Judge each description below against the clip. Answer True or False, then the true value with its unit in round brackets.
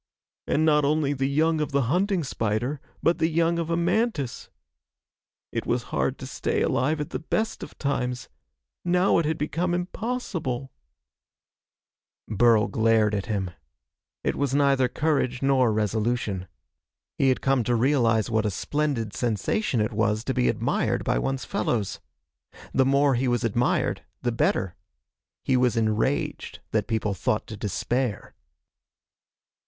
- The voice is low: True (130 Hz)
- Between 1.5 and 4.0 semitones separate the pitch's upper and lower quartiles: False (5.1 semitones)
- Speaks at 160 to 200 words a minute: False (150 wpm)